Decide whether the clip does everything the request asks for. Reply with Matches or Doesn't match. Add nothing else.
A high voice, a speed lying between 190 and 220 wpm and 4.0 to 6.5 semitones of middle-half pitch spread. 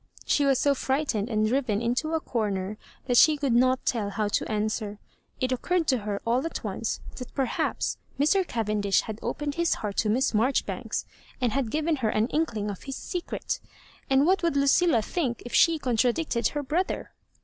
Matches